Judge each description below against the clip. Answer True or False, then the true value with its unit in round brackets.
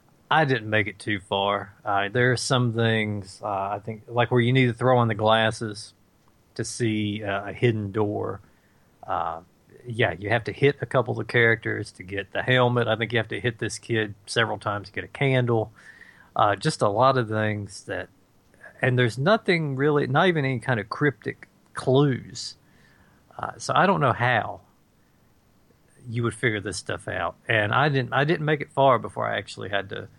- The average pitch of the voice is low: True (115 Hz)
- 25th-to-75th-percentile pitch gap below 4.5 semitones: True (3.5 semitones)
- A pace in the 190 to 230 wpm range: True (200 wpm)